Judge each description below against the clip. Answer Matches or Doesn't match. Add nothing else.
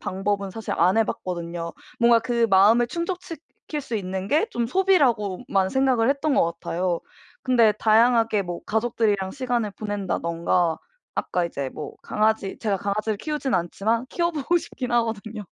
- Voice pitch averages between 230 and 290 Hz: Doesn't match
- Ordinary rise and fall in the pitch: Matches